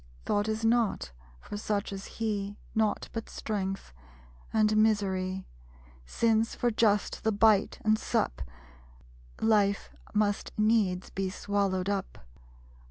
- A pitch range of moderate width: No, narrow, 1.8 semitones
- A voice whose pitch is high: Yes, high, 205 Hz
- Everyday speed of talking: No, slow, 115 wpm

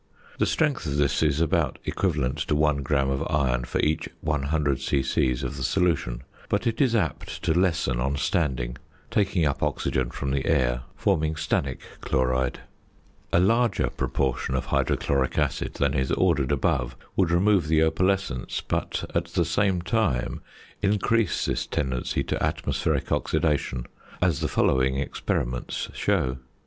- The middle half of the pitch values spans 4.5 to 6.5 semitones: Yes, average, 4.8 semitones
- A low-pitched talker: Yes, very low, 75 Hz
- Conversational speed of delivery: Yes, average, 150 wpm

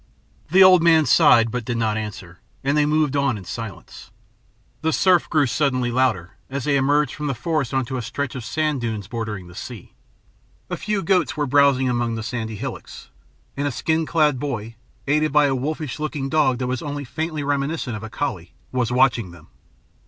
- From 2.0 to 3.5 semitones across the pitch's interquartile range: No, average, 4.2 semitones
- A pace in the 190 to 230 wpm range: Yes, average, 195 wpm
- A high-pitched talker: No, low, 135 Hz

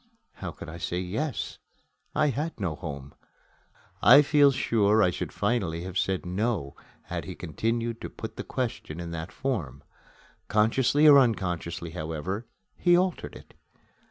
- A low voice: Yes, low, 100 Hz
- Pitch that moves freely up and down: Yes, wide, 7.0 semitones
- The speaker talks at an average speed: Yes, average, 150 wpm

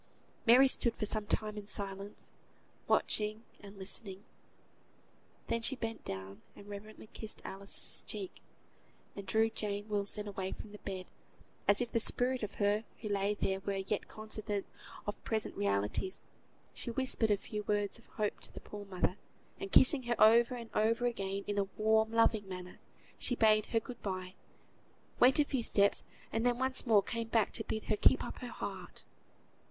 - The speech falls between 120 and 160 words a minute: No, average, 175 wpm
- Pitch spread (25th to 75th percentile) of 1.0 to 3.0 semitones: Yes, narrow, 2.4 semitones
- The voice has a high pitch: Yes, high, 210 Hz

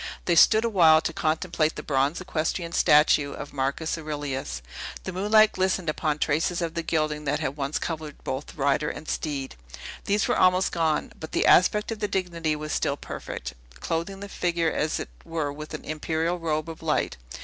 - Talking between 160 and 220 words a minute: Yes, average, 180 wpm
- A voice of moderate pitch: Yes, medium, 160 Hz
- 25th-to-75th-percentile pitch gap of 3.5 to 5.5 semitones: No, narrow, 2.6 semitones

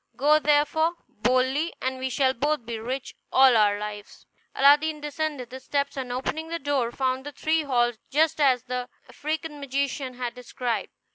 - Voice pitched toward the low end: No, very high, 265 Hz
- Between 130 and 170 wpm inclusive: Yes, average, 165 wpm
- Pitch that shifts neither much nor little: Yes, average, 3.1 semitones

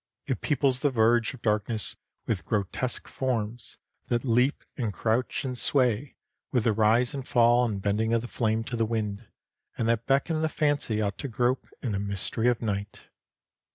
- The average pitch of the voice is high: No, low, 115 Hz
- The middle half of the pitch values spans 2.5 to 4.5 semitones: Yes, average, 2.8 semitones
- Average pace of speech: Yes, average, 180 wpm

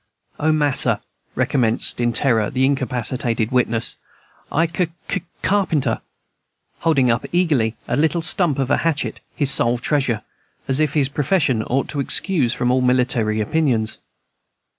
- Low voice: Yes, low, 130 Hz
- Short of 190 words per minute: Yes, average, 145 wpm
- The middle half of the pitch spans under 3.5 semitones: No, average, 4.3 semitones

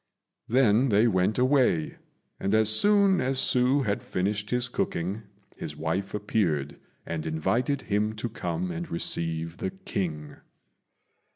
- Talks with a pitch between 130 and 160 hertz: No, low, 105 Hz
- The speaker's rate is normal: No, slow, 130 wpm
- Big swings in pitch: Yes, wide, 6.7 semitones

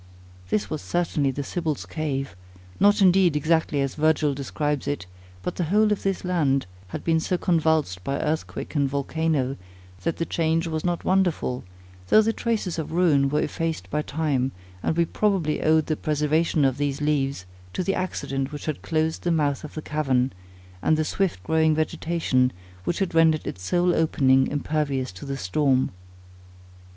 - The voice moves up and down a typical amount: Yes, average, 3.3 semitones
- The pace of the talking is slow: No, average, 170 wpm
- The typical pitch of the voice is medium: Yes, medium, 155 Hz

